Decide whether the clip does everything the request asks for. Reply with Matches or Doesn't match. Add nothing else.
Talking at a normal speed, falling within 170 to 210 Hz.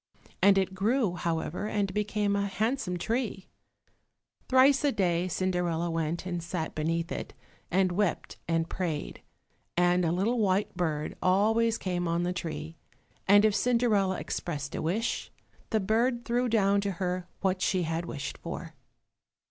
Matches